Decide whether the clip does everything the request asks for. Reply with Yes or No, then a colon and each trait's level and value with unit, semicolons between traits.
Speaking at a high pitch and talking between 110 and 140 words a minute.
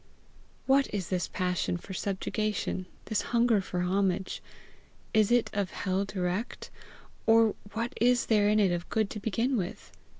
No: high, 205 Hz; average, 155 wpm